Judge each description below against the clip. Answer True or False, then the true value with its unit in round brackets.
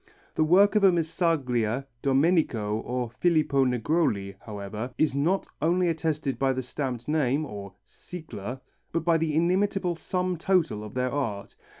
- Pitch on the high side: False (145 Hz)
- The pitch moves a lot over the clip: True (5.7 semitones)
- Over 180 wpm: False (145 wpm)